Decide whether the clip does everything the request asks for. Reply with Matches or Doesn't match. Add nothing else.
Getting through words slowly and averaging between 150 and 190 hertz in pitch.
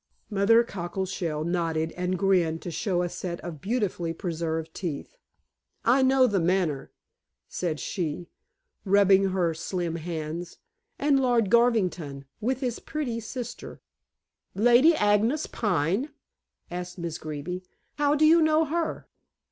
Matches